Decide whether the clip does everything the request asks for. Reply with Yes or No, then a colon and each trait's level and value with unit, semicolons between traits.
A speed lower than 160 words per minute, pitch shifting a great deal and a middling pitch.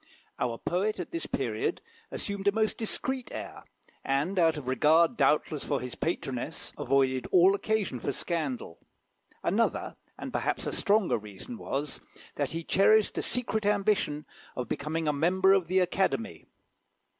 Yes: average, 150 wpm; wide, 6.3 semitones; medium, 170 Hz